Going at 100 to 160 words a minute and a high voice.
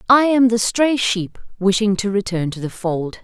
No: fast, 205 wpm; high, 210 Hz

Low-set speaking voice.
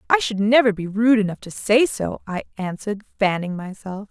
No: high, 210 Hz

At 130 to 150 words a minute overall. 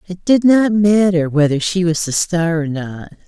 No: average, 200 wpm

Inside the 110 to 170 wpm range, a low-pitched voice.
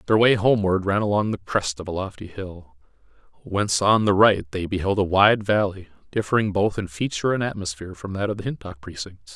No: fast, 205 wpm; very low, 95 Hz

